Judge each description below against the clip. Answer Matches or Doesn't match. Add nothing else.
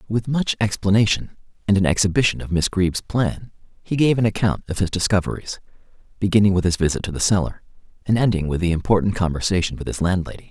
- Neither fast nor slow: Matches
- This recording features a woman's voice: Doesn't match